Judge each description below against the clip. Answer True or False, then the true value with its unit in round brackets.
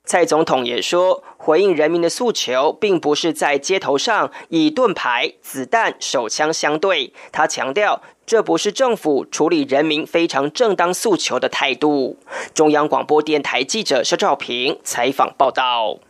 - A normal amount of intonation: False (6.6 semitones)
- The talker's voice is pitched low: False (165 Hz)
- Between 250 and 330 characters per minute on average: False (240 characters per minute)